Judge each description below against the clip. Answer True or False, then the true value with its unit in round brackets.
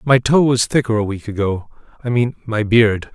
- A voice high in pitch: False (115 Hz)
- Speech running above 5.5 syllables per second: False (5.0 syllables/s)